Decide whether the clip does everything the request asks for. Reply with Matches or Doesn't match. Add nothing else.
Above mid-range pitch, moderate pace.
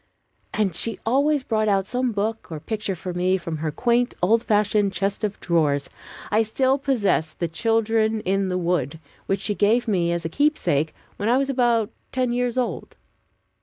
Matches